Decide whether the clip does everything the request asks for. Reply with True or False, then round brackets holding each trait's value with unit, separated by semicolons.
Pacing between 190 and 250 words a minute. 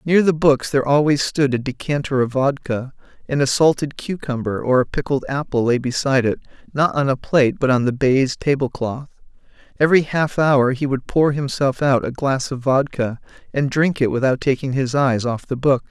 True (200 wpm)